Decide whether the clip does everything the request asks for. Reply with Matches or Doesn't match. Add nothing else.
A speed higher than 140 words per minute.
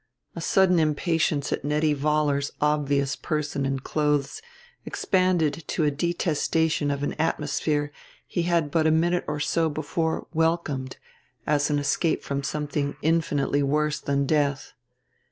Doesn't match